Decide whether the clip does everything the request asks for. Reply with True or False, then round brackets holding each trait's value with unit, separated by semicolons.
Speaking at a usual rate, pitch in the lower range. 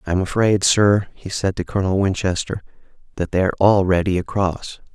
True (145 wpm; 95 Hz)